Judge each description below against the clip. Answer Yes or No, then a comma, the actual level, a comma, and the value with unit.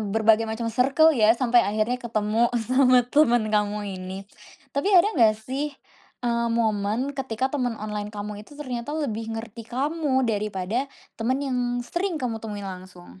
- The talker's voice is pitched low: No, high, 235 Hz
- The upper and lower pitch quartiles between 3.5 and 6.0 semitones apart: Yes, average, 3.8 semitones